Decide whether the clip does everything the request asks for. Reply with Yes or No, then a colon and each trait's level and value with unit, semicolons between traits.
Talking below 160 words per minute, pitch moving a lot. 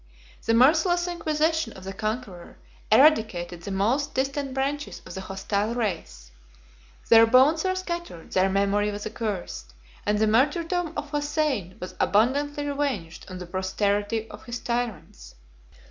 Yes: average, 140 wpm; wide, 7.0 semitones